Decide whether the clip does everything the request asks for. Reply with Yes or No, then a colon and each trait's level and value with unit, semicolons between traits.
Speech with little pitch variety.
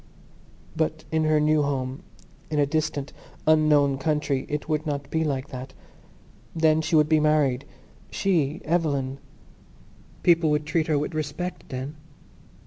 Yes: narrow, 1.9 semitones